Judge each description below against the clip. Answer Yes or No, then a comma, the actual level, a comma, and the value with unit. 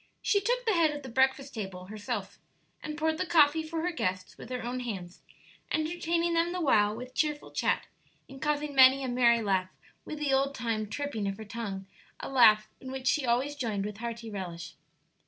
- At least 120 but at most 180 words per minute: No, average, 200 wpm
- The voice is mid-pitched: No, very high, 255 Hz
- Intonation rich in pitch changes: Yes, wide, 5.8 semitones